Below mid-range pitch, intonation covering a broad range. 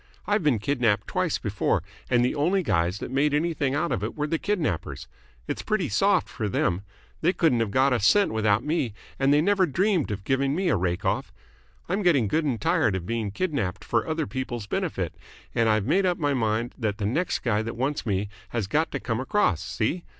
Yes: low, 130 Hz; wide, 7.0 semitones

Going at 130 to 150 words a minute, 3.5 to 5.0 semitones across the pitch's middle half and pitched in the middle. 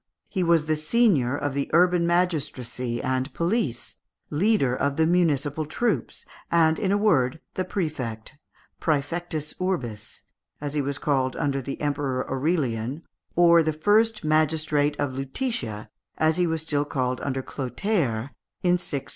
Yes: average, 145 wpm; average, 4.4 semitones; medium, 150 Hz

